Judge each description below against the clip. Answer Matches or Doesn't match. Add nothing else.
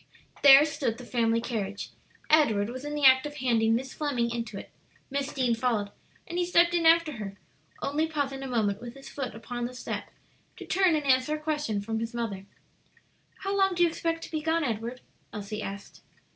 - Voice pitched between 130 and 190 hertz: Doesn't match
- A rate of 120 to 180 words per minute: Doesn't match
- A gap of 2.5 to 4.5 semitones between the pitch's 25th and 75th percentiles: Doesn't match